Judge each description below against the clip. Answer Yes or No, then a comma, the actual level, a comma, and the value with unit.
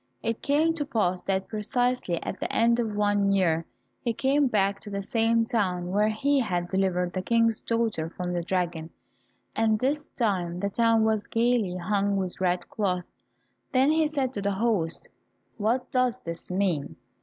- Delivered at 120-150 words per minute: No, average, 175 wpm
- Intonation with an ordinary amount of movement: Yes, average, 4.2 semitones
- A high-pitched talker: Yes, high, 210 Hz